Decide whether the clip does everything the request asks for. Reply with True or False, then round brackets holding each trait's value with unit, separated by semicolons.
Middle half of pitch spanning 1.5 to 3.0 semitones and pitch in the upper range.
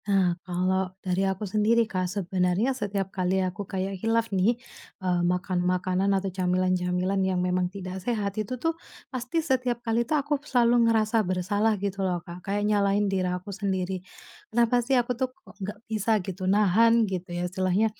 False (3.6 semitones; 195 Hz)